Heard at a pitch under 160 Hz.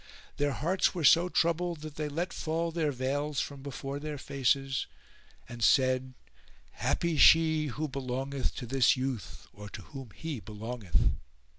Yes: medium, 140 Hz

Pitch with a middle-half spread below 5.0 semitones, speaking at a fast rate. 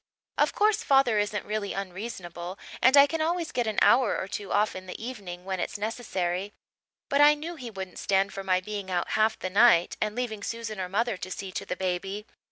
Yes: average, 4.3 semitones; fast, 215 wpm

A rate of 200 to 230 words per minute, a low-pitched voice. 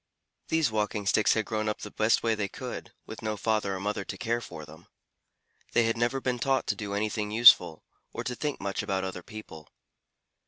Yes: fast, 205 wpm; low, 110 Hz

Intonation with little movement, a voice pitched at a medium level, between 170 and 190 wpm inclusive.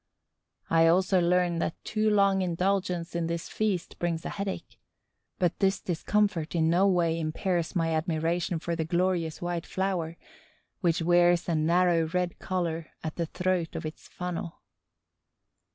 No: narrow, 1.9 semitones; medium, 175 Hz; average, 150 wpm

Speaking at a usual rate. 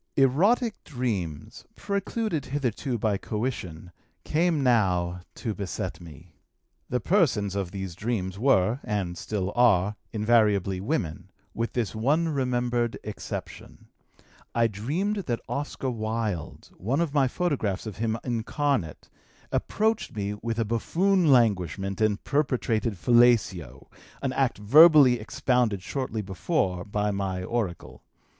No: slow, 120 wpm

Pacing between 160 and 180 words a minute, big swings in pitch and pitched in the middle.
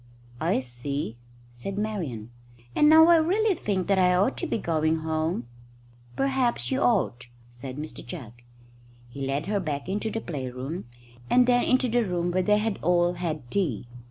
Yes: average, 170 wpm; wide, 7.6 semitones; medium, 175 Hz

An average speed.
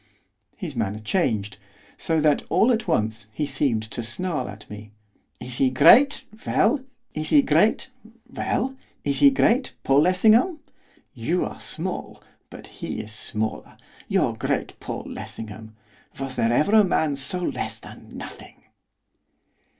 No: slow, 130 wpm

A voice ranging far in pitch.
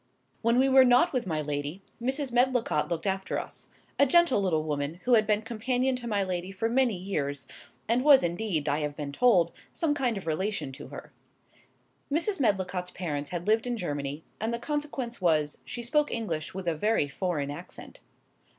Yes: wide, 7.7 semitones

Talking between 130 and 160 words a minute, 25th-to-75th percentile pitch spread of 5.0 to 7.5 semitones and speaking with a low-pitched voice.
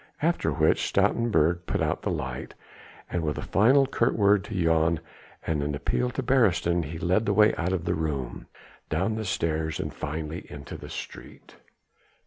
No: average, 175 wpm; wide, 5.5 semitones; very low, 85 Hz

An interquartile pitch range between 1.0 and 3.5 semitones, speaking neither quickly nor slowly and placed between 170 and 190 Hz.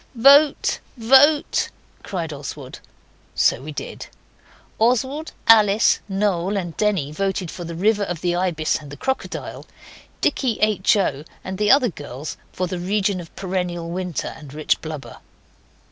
No: average, 4.4 semitones; average, 145 wpm; medium, 185 Hz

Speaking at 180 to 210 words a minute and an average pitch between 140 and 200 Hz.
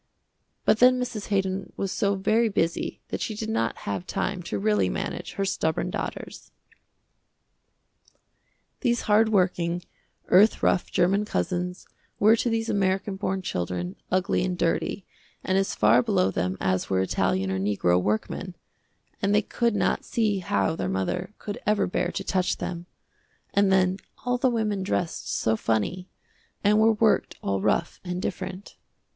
No: average, 155 wpm; high, 190 Hz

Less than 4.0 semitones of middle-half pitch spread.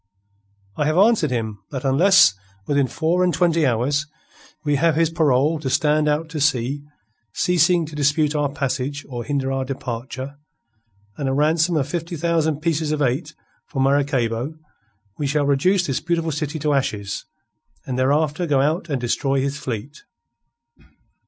Yes: average, 3.0 semitones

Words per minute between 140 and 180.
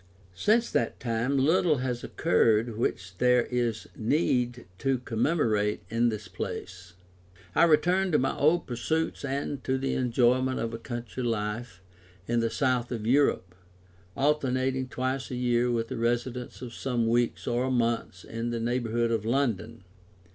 Yes: average, 150 wpm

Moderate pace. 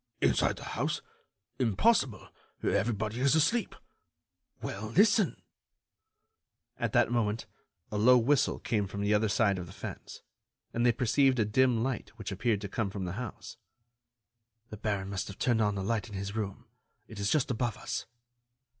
Yes: average, 165 wpm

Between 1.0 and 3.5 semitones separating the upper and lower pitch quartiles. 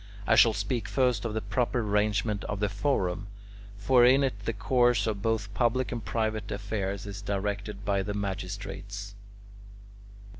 Yes: narrow, 2.4 semitones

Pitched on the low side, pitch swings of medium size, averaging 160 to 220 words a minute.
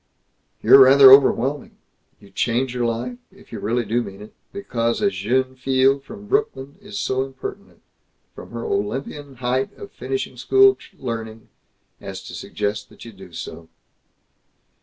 No: low, 125 Hz; average, 3.3 semitones; average, 150 wpm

